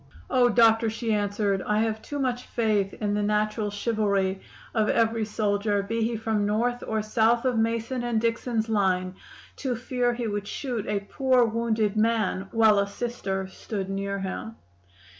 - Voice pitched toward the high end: Yes, high, 220 Hz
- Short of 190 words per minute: Yes, average, 165 wpm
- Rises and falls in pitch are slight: Yes, narrow, 2.2 semitones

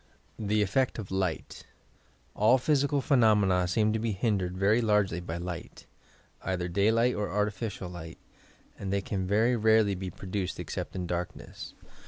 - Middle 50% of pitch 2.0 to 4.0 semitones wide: Yes, average, 3.2 semitones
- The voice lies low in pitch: Yes, low, 100 Hz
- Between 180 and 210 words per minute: No, average, 155 wpm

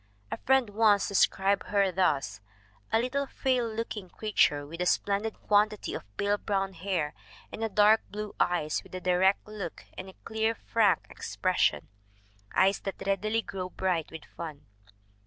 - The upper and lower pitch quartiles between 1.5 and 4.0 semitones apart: Yes, average, 3.0 semitones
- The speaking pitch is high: Yes, high, 200 Hz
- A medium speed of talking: Yes, average, 155 wpm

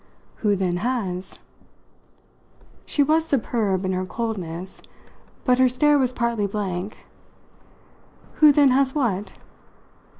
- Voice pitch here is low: No, high, 225 Hz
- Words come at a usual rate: No, slow, 110 wpm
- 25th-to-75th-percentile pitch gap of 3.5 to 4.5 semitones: No, wide, 5.6 semitones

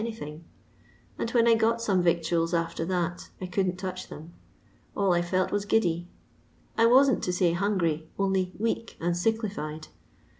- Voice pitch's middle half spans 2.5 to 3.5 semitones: No, average, 4.4 semitones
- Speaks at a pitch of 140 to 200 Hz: Yes, medium, 185 Hz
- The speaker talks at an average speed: Yes, average, 155 wpm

